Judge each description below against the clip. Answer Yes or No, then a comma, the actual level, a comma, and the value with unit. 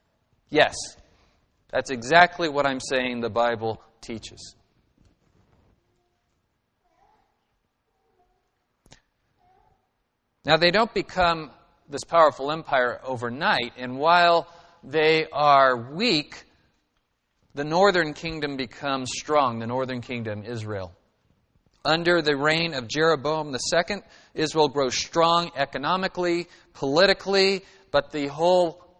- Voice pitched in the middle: Yes, medium, 150 Hz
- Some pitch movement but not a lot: No, wide, 5.8 semitones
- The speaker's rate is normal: No, slow, 95 wpm